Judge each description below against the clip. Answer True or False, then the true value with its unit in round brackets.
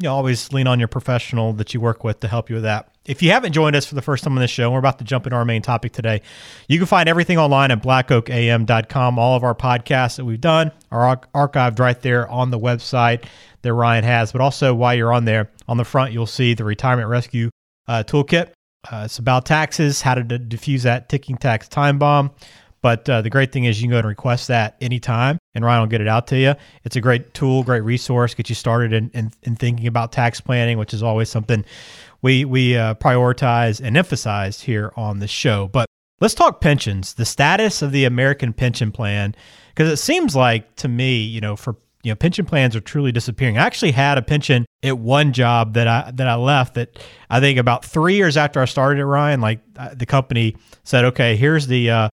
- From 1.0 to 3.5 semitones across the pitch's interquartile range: True (2.8 semitones)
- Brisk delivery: True (230 wpm)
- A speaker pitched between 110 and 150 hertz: True (125 Hz)